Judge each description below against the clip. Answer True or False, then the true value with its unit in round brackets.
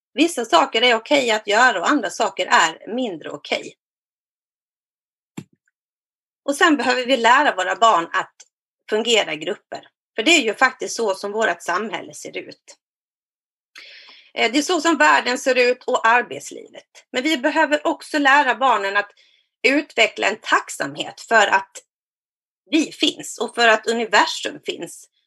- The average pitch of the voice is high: True (250 Hz)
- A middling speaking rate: True (150 wpm)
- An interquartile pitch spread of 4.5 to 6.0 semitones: True (5.5 semitones)